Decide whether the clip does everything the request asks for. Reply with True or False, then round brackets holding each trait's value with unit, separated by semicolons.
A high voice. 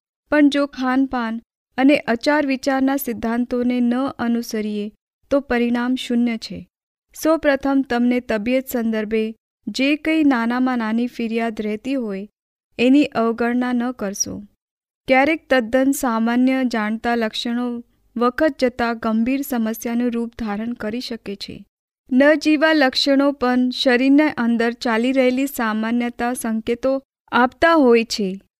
True (245 Hz)